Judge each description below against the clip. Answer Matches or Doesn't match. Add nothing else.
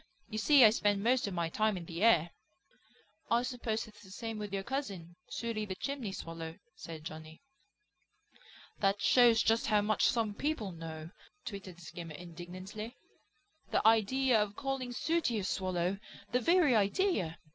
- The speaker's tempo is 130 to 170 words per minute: Matches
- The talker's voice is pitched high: Matches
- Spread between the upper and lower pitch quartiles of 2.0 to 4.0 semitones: Doesn't match